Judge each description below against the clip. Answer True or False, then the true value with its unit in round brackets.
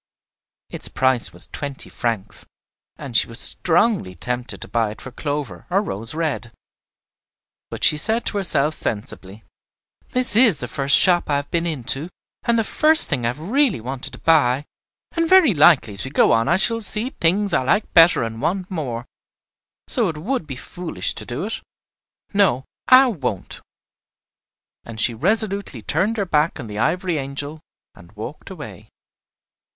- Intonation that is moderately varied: False (8.1 semitones)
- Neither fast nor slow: True (170 wpm)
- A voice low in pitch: False (150 Hz)